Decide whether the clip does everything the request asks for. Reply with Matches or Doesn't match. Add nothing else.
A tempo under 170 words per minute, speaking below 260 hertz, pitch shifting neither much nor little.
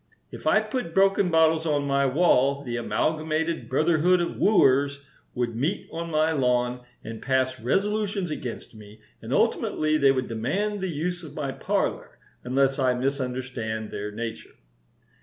Matches